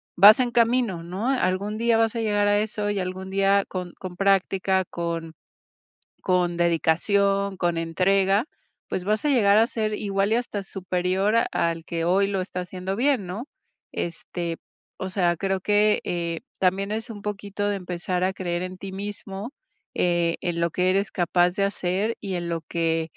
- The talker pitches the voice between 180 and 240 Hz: Yes, high, 190 Hz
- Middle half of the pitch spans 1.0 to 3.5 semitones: Yes, narrow, 2.6 semitones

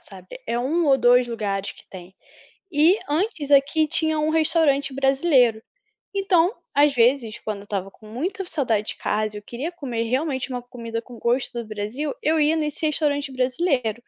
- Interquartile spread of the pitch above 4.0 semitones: Yes, average, 4.9 semitones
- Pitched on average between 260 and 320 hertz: Yes, very high, 270 Hz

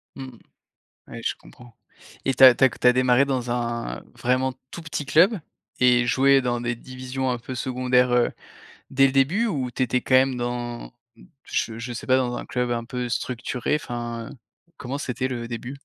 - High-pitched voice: No, low, 125 Hz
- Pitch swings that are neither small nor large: No, narrow, 1.6 semitones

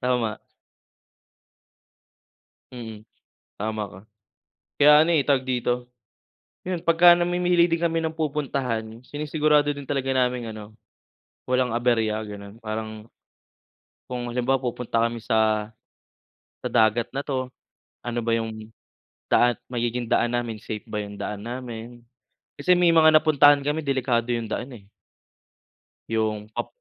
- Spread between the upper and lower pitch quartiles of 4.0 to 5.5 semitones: Yes, average, 4.5 semitones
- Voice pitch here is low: Yes, low, 120 Hz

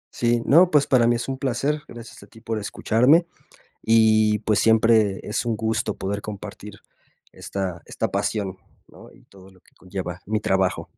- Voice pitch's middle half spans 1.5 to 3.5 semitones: Yes, average, 3.1 semitones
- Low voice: Yes, low, 110 Hz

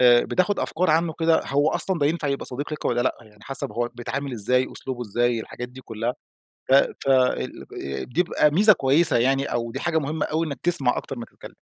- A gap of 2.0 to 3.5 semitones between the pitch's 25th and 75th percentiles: No, average, 4.6 semitones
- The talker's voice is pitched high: No, low, 135 Hz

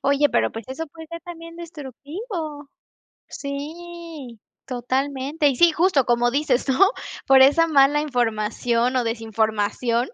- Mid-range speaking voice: No, very high, 280 Hz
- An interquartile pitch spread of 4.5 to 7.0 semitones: Yes, average, 4.9 semitones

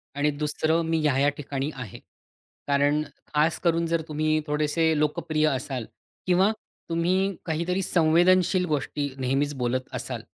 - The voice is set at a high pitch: No, medium, 155 Hz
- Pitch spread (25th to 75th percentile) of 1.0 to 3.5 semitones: Yes, average, 2.7 semitones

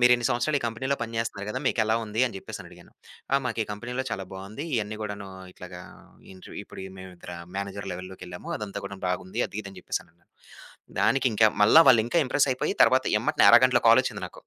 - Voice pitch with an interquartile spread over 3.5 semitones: Yes, average, 4.1 semitones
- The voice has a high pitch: No, low, 105 Hz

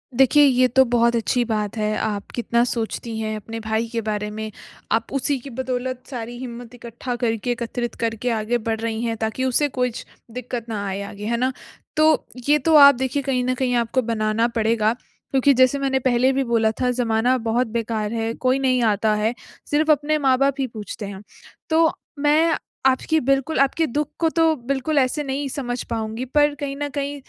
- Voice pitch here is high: Yes, high, 245 Hz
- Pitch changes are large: No, average, 3.2 semitones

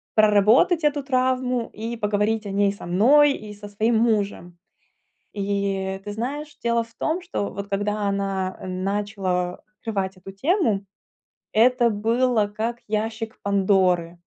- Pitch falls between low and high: No, high, 210 Hz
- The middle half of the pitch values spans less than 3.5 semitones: Yes, average, 3.1 semitones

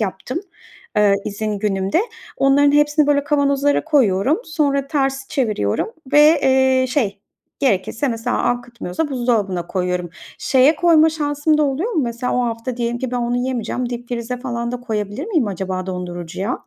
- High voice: Yes, very high, 250 Hz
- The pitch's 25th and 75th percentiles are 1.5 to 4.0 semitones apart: No, average, 5.3 semitones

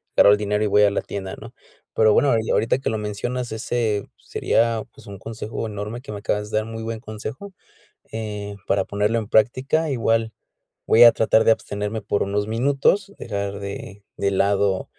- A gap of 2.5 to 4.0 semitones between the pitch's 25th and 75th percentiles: No, narrow, 2.0 semitones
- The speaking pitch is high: No, low, 110 Hz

